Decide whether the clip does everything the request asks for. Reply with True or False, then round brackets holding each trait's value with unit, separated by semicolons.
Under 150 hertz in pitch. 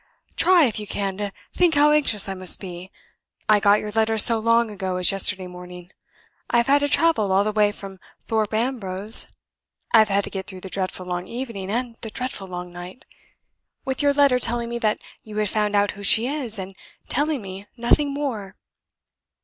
False (210 Hz)